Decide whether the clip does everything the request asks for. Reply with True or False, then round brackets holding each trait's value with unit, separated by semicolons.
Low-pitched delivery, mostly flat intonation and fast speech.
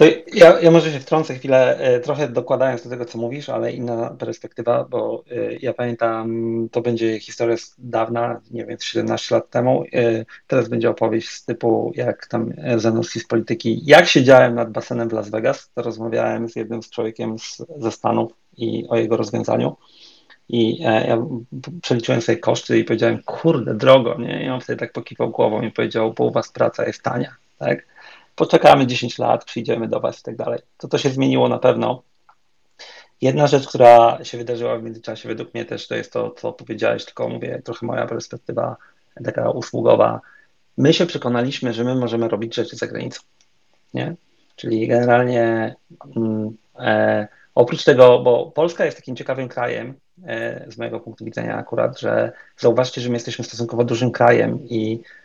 True (120 Hz; 1.6 semitones; 170 wpm)